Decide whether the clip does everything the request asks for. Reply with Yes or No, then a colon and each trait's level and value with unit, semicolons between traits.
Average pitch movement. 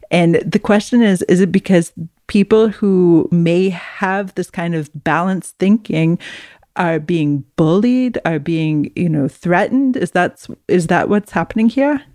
Yes: average, 3.8 semitones